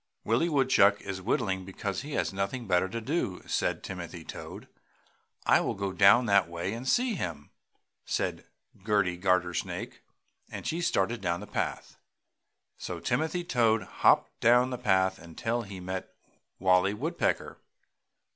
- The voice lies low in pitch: Yes, low, 100 Hz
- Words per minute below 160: Yes, average, 145 wpm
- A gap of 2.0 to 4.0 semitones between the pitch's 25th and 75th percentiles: No, average, 4.7 semitones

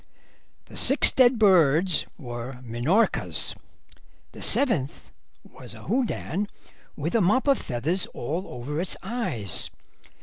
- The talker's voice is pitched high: No, medium, 170 Hz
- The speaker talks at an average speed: No, slow, 115 wpm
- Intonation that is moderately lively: No, wide, 8.8 semitones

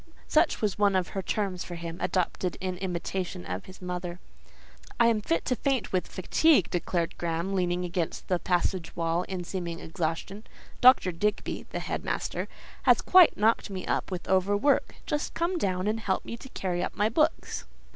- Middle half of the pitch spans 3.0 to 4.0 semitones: Yes, average, 3.3 semitones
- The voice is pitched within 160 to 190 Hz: Yes, medium, 185 Hz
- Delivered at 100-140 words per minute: No, average, 175 wpm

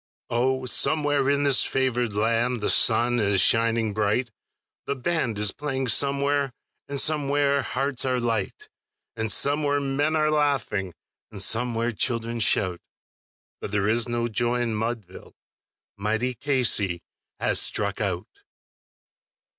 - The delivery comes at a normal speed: No, slow, 130 wpm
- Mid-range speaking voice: No, low, 120 Hz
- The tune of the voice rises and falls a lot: No, average, 3.9 semitones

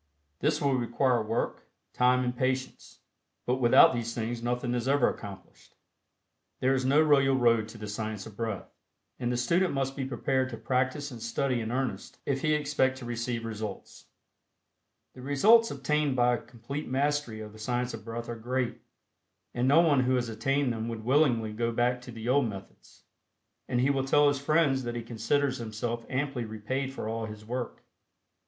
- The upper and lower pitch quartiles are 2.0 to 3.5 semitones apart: Yes, average, 2.8 semitones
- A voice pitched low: Yes, low, 125 Hz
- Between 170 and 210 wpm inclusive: Yes, average, 185 wpm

